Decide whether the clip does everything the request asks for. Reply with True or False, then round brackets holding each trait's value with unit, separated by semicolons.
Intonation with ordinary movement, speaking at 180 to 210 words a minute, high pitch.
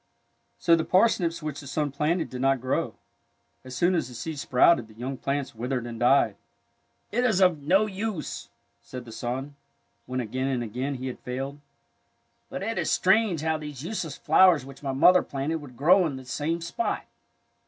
False (4.8 semitones; 190 wpm; 140 Hz)